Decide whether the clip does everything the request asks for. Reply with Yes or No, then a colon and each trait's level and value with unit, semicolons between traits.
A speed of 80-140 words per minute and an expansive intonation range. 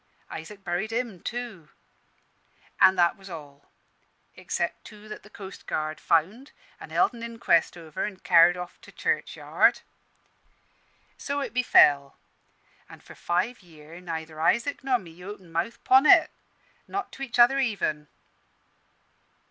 Yes: slow, 135 wpm; wide, 6.2 semitones